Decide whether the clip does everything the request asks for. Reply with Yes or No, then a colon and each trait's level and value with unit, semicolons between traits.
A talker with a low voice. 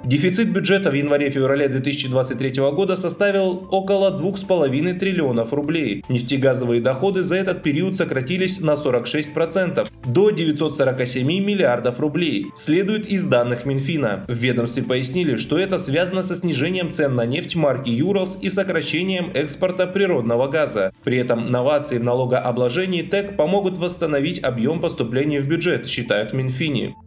No: medium, 150 Hz